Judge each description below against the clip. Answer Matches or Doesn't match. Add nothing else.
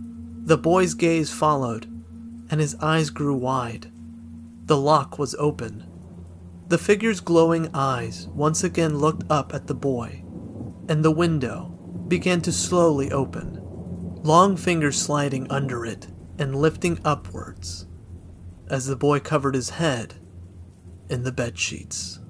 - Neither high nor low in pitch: Doesn't match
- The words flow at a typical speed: Doesn't match